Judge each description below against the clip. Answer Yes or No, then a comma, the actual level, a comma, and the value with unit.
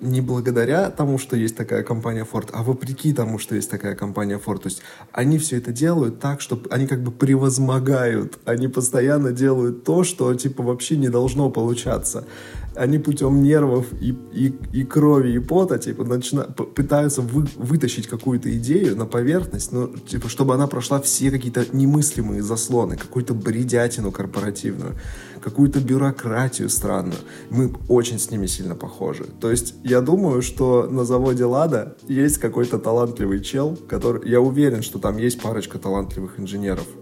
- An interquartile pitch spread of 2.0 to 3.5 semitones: Yes, average, 2.9 semitones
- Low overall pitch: Yes, low, 125 Hz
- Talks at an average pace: Yes, average, 160 wpm